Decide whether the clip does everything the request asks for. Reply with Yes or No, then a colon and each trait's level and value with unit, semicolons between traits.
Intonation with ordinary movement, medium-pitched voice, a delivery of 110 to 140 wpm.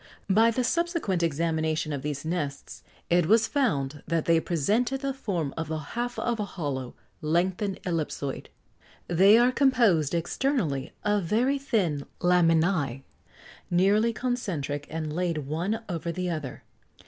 No: wide, 6.3 semitones; medium, 175 Hz; slow, 135 wpm